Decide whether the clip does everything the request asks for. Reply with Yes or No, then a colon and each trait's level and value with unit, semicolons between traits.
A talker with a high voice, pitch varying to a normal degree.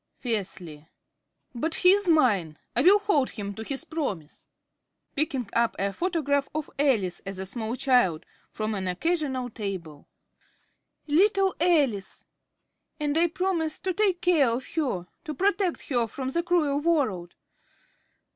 No: very high, 275 Hz; wide, 8.6 semitones